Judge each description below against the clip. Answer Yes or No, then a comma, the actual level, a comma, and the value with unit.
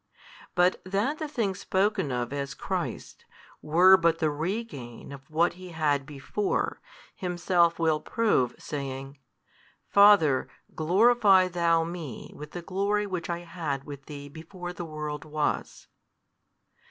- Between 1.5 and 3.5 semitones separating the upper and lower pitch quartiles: No, average, 4.3 semitones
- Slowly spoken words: Yes, slow, 130 wpm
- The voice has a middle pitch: Yes, medium, 170 Hz